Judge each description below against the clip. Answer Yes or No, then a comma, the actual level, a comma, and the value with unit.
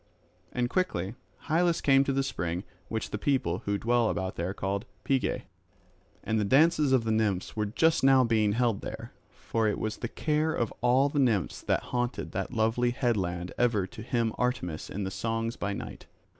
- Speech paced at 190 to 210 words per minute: No, average, 180 wpm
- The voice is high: No, low, 115 Hz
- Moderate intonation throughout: Yes, average, 4.5 semitones